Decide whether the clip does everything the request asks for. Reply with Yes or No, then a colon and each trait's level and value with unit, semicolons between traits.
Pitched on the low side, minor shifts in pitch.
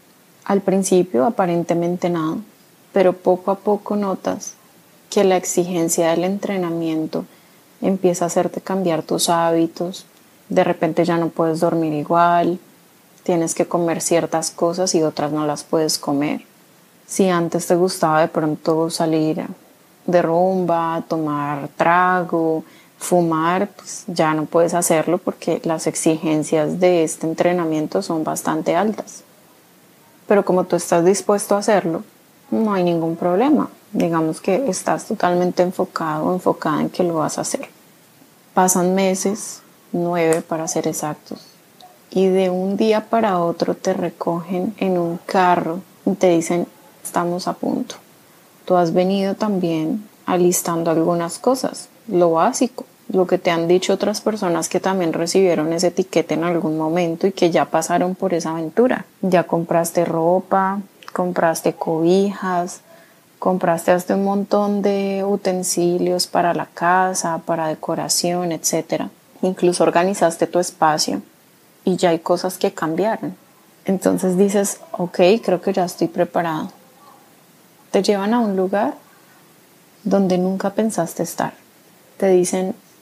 No: medium, 175 Hz; narrow, 2.3 semitones